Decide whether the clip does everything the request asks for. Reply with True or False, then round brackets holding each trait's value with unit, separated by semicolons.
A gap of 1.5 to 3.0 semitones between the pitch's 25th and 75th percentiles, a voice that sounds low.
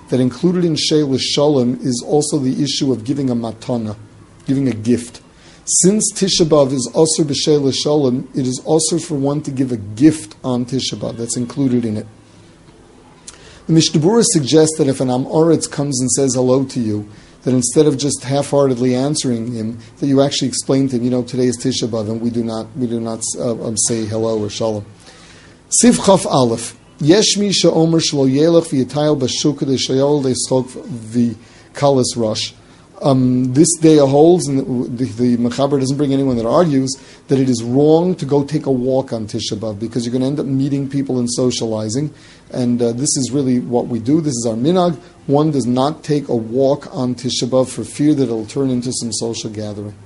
False (3.5 semitones; 130 Hz)